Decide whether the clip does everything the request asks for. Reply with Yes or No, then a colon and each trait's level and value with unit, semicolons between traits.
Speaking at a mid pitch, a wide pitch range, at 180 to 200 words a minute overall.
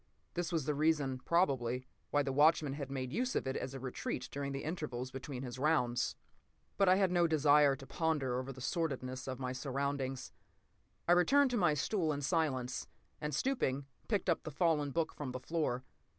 No: medium, 145 Hz; average, 3.8 semitones; average, 195 wpm